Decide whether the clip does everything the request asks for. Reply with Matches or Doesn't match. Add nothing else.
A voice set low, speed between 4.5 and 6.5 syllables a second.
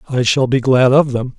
Matches